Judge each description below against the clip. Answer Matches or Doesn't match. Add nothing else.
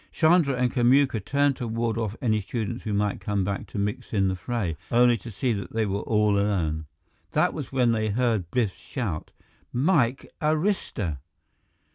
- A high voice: Doesn't match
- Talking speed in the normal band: Matches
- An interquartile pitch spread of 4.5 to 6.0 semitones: Doesn't match